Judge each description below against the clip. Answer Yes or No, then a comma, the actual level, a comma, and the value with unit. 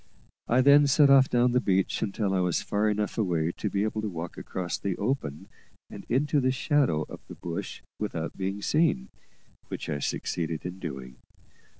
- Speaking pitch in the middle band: No, low, 100 Hz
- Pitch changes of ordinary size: No, wide, 6.7 semitones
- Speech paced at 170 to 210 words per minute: Yes, average, 185 wpm